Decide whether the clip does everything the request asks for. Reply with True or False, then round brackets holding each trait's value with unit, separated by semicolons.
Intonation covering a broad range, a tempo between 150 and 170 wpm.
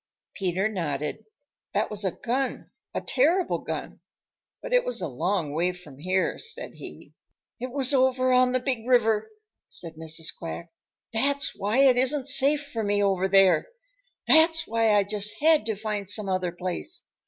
True (6.0 semitones; 165 wpm)